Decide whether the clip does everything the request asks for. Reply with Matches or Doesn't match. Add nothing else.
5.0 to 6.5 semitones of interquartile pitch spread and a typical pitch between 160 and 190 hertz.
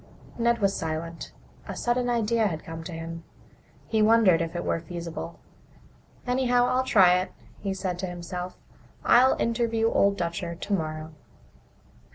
Matches